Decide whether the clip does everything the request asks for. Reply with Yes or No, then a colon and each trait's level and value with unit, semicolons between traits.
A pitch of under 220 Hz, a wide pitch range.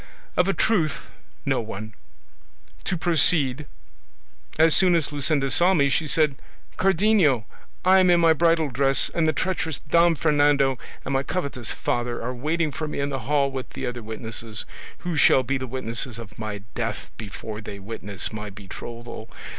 Yes: medium, 140 Hz; wide, 5.7 semitones